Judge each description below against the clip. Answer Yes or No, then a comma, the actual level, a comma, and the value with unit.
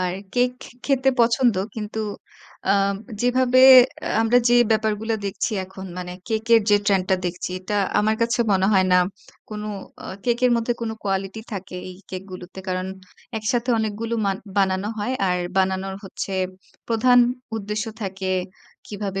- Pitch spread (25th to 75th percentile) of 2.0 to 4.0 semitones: Yes, average, 3.3 semitones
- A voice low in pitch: No, high, 210 Hz